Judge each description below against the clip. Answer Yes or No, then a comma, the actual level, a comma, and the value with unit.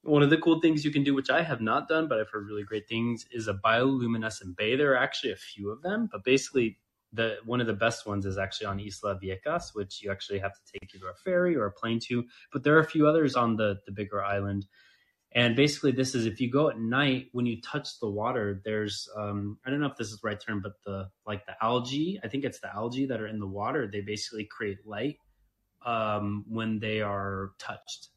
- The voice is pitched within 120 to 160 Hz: No, low, 110 Hz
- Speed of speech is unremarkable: No, fast, 245 wpm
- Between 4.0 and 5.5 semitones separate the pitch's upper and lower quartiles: Yes, average, 4.5 semitones